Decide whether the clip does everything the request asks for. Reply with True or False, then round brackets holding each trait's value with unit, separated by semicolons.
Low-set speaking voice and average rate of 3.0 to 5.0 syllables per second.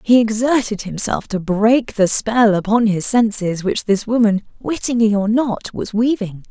False (220 Hz; 4.5 syllables/s)